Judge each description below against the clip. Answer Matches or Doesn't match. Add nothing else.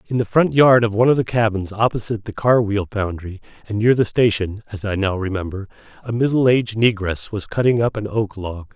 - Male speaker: Matches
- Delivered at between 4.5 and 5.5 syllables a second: Doesn't match